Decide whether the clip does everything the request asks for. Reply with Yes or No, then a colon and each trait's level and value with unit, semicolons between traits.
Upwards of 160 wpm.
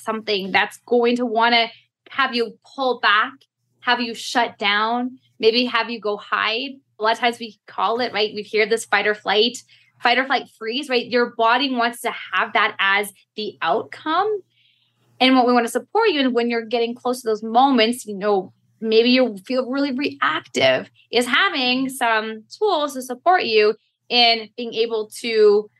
Yes: average, 185 wpm